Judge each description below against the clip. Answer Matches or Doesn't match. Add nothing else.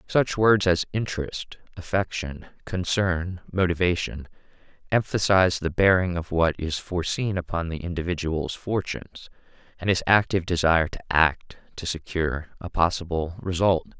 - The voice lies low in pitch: Matches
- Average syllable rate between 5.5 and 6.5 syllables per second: Doesn't match